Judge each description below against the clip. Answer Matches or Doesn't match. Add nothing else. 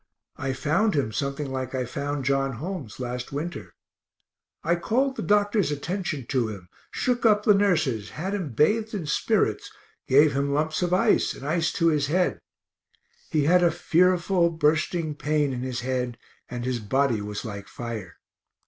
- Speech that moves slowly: Doesn't match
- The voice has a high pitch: Doesn't match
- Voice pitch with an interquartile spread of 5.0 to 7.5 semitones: Matches